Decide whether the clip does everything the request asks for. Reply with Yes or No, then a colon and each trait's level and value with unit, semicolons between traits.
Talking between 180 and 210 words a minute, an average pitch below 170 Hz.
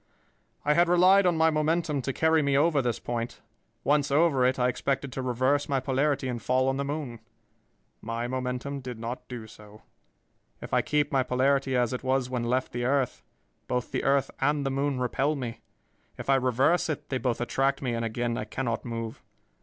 Yes: average, 200 wpm; low, 135 Hz